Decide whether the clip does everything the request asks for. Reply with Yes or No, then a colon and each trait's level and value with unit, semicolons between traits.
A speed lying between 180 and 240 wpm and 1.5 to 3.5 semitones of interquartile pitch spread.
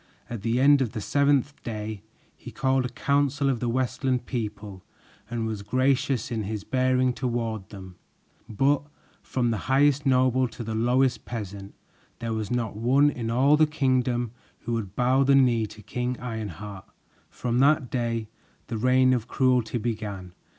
No: average, 165 wpm; average, 3.0 semitones